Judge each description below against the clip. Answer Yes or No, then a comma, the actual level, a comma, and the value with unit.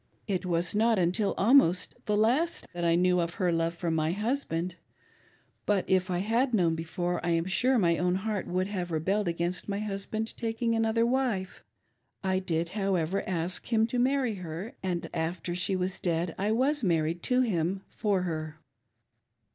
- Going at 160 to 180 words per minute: Yes, average, 175 wpm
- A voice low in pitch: No, medium, 185 Hz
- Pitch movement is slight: No, average, 4.3 semitones